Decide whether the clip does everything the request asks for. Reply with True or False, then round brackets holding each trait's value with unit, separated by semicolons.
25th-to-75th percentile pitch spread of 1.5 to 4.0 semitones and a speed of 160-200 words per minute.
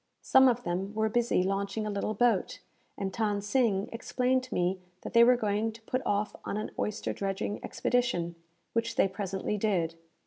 True (3.1 semitones; 180 wpm)